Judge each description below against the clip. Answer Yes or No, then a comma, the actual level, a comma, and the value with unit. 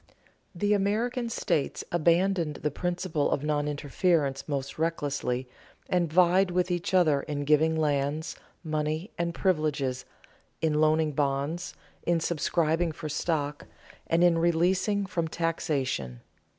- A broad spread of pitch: No, average, 3.1 semitones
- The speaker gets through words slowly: Yes, slow, 125 wpm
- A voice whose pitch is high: No, medium, 160 Hz